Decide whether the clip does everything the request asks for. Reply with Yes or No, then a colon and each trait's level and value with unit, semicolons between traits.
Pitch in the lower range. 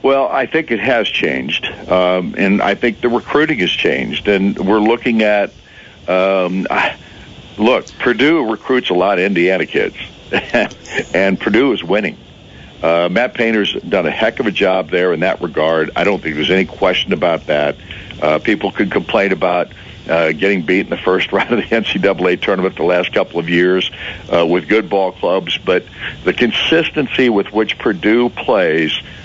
Yes: very low, 95 Hz